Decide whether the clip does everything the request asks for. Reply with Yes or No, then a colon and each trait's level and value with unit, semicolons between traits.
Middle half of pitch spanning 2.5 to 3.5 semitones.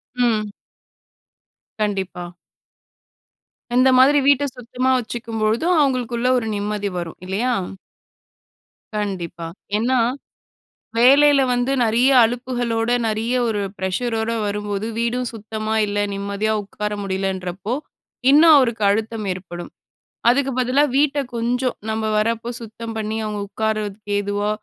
Yes: average, 3.2 semitones